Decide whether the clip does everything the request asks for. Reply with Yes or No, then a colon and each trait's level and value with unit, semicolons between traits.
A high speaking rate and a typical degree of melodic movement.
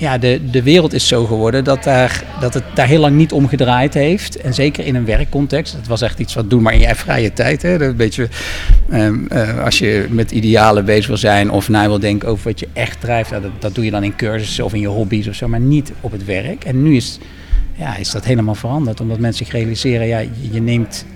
Yes: fast, 255 wpm; average, 3.5 semitones